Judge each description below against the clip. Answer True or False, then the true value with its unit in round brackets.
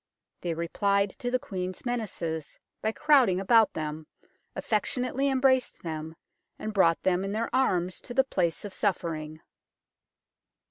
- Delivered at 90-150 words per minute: True (140 wpm)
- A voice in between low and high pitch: False (195 Hz)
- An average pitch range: False (6.4 semitones)